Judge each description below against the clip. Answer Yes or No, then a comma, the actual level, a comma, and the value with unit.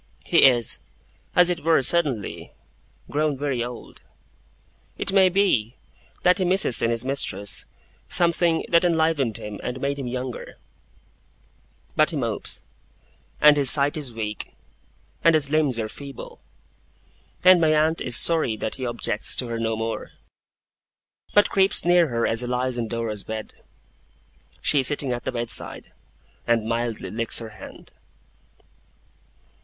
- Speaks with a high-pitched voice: No, low, 130 Hz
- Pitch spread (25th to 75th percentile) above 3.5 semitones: Yes, wide, 5.5 semitones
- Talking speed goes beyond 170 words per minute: No, average, 145 wpm